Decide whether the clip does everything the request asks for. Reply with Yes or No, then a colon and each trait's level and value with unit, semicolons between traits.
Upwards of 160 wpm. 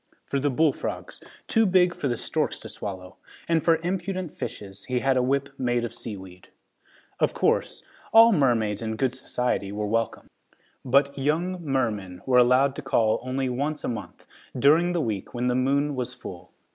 Yes: average, 180 wpm